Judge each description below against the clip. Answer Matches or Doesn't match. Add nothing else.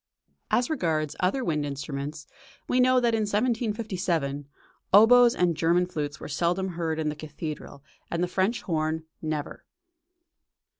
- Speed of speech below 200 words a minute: Matches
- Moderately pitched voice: Matches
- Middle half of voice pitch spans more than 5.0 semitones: Matches